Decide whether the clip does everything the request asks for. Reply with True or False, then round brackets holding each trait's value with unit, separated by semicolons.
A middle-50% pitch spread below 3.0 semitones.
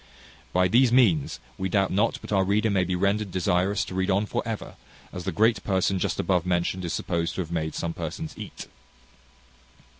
True (2.5 semitones)